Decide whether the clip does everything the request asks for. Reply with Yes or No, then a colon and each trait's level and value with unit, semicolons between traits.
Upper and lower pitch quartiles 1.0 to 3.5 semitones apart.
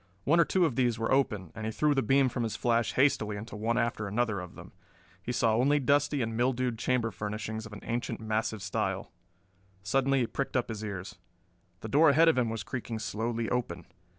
Yes: average, 3.2 semitones